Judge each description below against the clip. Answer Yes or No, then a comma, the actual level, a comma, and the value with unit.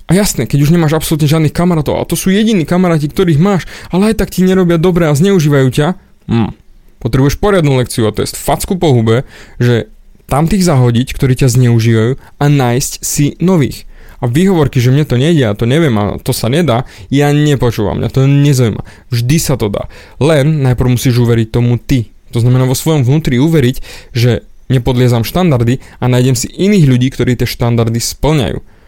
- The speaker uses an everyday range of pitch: Yes, average, 5.0 semitones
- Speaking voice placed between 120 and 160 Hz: Yes, low, 135 Hz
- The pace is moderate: No, fast, 185 wpm